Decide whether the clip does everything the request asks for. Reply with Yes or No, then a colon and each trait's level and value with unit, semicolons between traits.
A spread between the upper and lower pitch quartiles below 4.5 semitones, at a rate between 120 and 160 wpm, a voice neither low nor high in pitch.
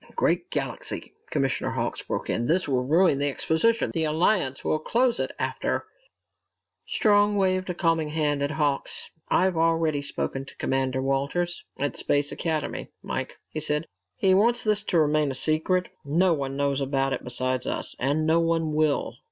No: average, 3.9 semitones; average, 170 wpm; medium, 155 Hz